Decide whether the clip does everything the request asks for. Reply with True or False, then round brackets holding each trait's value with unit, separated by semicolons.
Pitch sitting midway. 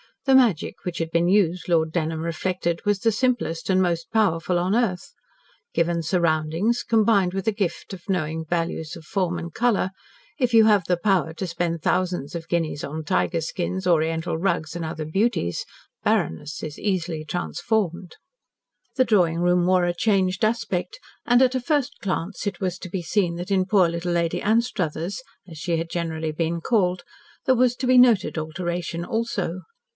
True (175 Hz)